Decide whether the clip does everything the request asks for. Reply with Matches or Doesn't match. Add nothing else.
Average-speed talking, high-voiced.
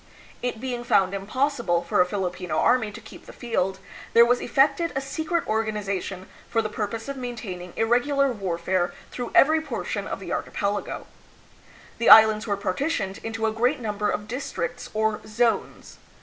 Matches